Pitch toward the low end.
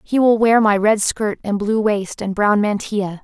No: high, 210 Hz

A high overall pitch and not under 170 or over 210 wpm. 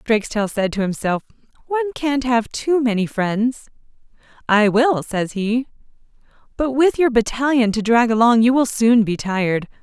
No: high, 235 Hz; average, 160 wpm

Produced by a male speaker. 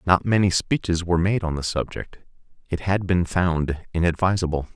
Yes: male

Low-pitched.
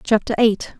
No: high, 220 Hz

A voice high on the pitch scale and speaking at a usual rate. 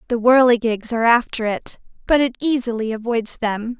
Yes: high, 235 Hz; average, 160 wpm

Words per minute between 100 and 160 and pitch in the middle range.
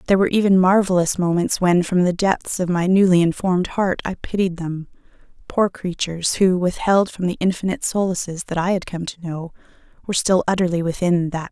No: average, 180 wpm; medium, 180 Hz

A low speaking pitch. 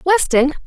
No: very high, 310 Hz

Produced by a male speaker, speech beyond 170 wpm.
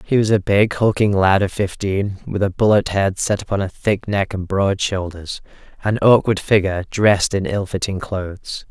Yes: male; average, 185 wpm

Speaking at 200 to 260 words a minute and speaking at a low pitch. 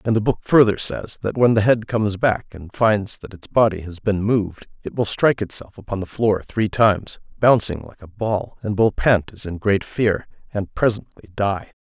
Yes: fast, 205 wpm; low, 105 Hz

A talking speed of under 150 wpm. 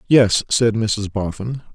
Yes: slow, 135 wpm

